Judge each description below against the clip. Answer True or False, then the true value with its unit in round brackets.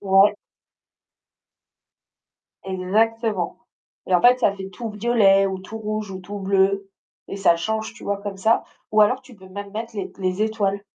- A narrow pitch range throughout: True (2.2 semitones)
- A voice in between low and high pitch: False (200 Hz)